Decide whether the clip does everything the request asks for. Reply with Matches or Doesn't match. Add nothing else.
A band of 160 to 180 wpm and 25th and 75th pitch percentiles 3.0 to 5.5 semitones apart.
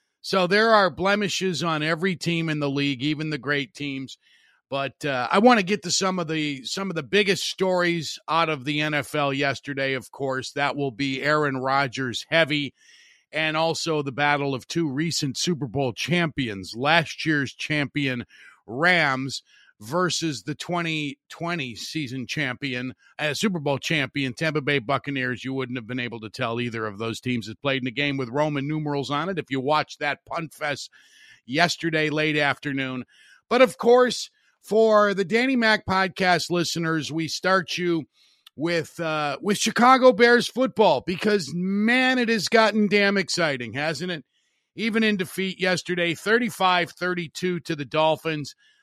Matches